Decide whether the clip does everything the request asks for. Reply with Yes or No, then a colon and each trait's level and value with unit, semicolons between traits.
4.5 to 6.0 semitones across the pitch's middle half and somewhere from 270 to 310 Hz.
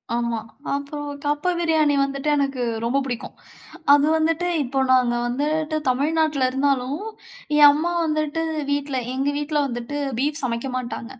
No: average, 2.9 semitones; very high, 285 Hz